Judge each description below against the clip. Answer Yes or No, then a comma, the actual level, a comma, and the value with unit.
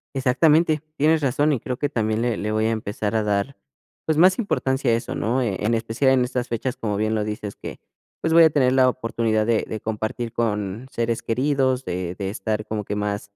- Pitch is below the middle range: Yes, low, 115 Hz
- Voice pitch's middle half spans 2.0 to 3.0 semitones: No, average, 3.6 semitones